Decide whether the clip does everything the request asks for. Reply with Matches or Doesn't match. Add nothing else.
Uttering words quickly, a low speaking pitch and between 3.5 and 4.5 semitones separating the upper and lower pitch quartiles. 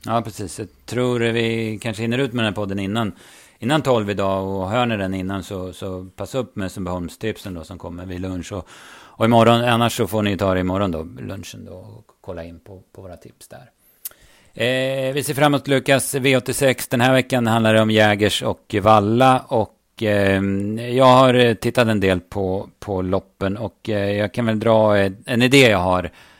Matches